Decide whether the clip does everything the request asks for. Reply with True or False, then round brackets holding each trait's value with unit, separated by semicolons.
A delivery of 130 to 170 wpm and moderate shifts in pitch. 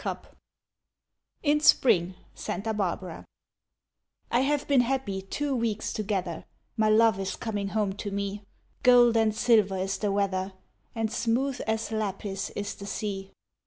True (140 wpm; 3.0 semitones)